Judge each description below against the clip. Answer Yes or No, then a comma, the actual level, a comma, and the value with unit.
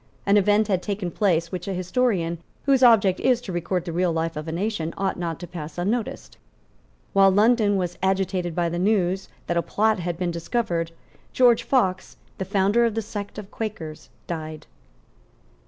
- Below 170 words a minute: No, average, 180 wpm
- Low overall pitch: No, high, 190 Hz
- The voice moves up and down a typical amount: Yes, average, 3.6 semitones